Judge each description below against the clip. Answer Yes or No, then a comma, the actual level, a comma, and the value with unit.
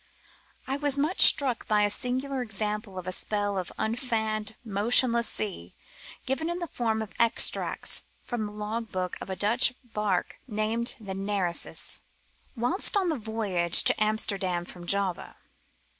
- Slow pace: No, average, 150 wpm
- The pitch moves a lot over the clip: No, average, 3.4 semitones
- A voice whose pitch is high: Yes, high, 215 Hz